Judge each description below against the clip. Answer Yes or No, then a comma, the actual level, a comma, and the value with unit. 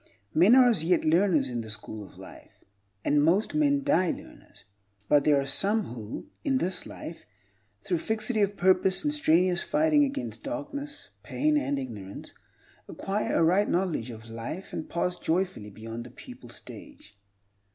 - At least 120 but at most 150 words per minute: No, average, 160 wpm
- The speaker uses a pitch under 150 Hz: No, medium, 180 Hz